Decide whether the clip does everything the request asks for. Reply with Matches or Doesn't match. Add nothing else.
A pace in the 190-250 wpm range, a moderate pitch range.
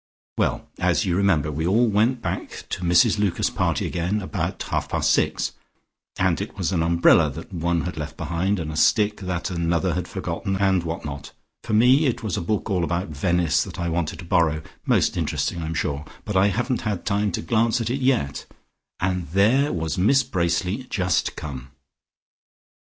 Matches